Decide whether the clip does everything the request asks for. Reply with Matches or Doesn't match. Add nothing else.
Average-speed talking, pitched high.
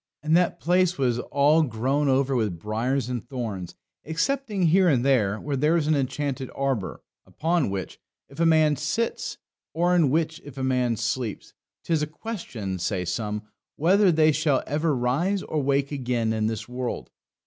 Doesn't match